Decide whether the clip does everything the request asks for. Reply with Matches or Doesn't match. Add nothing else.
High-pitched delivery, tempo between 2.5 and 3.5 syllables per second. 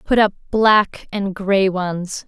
Matches